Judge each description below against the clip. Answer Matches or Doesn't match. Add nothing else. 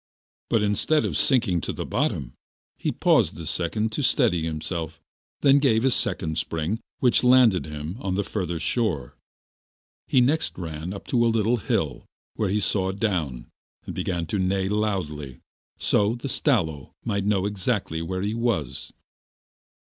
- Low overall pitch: Matches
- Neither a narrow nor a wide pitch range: Doesn't match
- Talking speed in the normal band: Matches